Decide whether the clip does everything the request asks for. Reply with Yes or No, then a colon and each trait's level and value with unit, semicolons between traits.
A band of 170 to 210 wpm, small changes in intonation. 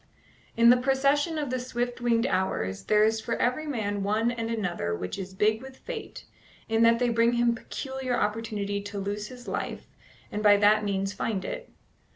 No: average, 190 wpm; average, 3.2 semitones